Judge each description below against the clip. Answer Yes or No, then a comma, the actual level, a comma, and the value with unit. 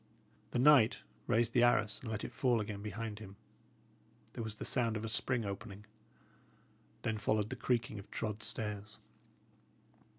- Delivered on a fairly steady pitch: Yes, narrow, 2.0 semitones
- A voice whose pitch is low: Yes, low, 110 Hz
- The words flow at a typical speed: Yes, average, 160 wpm